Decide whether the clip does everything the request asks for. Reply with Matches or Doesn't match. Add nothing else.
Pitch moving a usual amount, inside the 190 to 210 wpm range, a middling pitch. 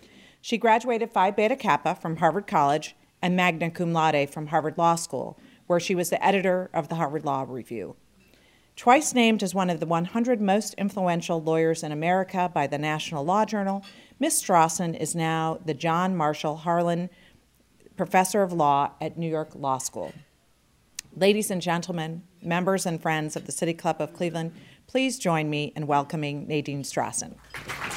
Doesn't match